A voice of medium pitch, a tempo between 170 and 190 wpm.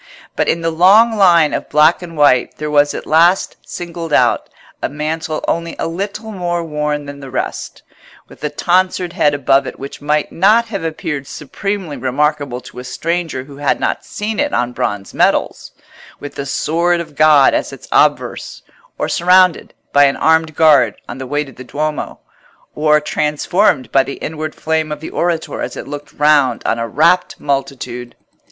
Yes: medium, 150 Hz; average, 180 wpm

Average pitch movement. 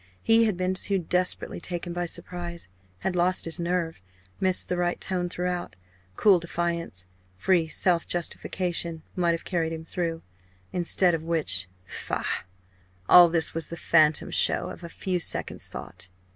No: narrow, 1.6 semitones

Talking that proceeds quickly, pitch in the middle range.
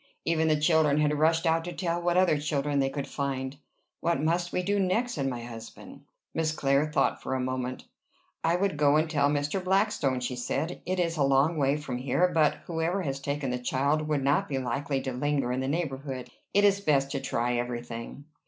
Yes: fast, 215 wpm; medium, 145 Hz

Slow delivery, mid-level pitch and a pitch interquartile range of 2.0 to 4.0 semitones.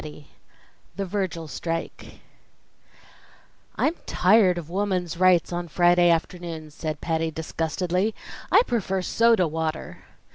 Yes: slow, 110 wpm; medium, 175 Hz; narrow, 2.5 semitones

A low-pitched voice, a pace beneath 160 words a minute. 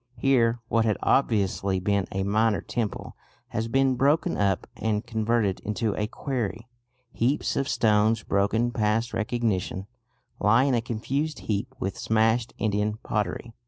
Yes: low, 110 Hz; average, 140 wpm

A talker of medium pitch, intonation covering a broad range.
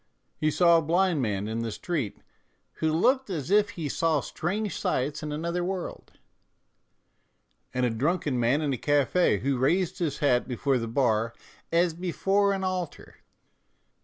Yes: medium, 155 Hz; wide, 5.7 semitones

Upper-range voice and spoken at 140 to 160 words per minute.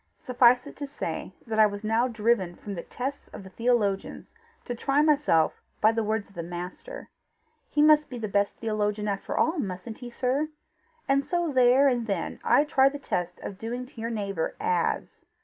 No: high, 230 Hz; average, 195 wpm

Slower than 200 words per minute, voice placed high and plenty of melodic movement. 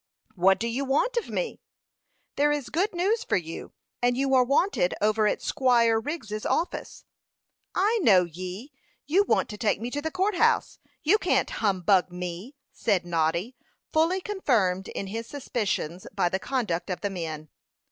Yes: average, 170 wpm; high, 230 Hz; wide, 8.1 semitones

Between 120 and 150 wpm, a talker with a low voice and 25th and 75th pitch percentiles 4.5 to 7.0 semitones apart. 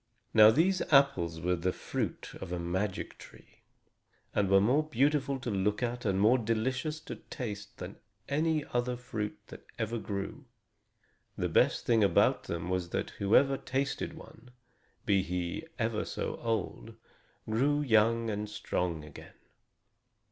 Yes: average, 140 wpm; low, 110 Hz; average, 5.1 semitones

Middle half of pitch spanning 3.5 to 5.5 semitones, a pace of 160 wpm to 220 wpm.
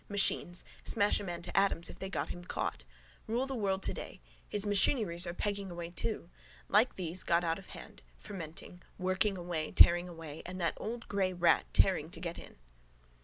No: average, 2.8 semitones; average, 185 wpm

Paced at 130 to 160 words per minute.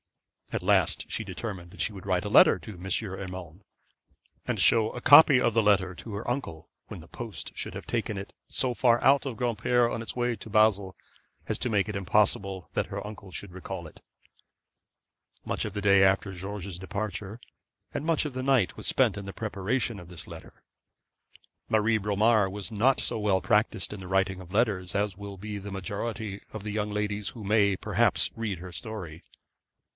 No: average, 195 wpm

